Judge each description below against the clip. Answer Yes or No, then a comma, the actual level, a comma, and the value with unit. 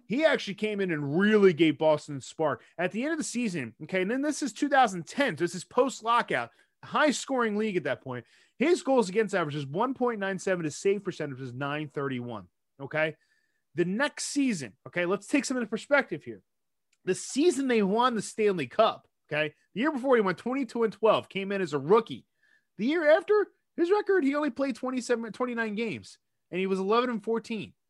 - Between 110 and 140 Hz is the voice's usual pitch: No, high, 215 Hz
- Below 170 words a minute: No, average, 195 wpm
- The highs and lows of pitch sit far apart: Yes, wide, 7.1 semitones